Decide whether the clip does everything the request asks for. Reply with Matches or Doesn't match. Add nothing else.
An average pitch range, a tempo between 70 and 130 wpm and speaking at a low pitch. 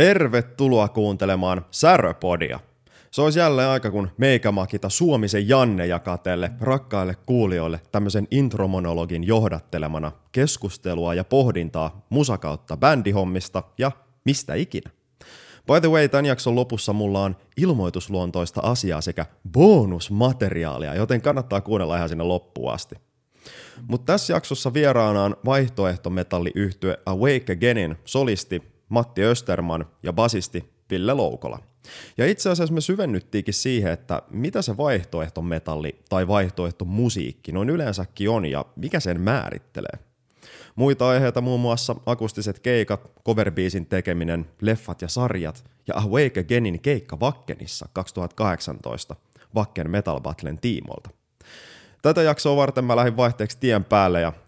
Doesn't match